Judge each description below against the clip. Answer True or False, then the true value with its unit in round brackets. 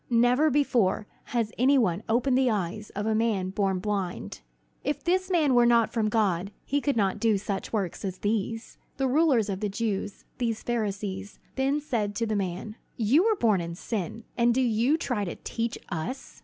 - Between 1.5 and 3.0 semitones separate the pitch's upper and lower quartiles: False (4.0 semitones)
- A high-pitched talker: True (225 Hz)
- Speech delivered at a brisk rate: False (190 wpm)